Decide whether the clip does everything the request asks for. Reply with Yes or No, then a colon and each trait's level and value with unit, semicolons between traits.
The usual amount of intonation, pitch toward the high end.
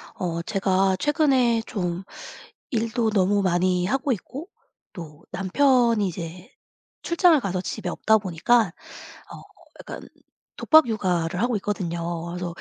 Yes: average, 5.0 semitones; high, 195 Hz